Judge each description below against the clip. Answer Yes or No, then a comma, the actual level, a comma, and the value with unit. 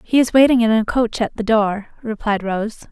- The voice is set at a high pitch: Yes, high, 220 Hz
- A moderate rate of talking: No, fast, 225 wpm